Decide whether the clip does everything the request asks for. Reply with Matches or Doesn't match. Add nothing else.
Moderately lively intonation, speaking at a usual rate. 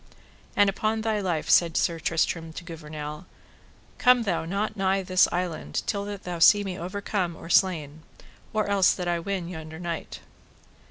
Matches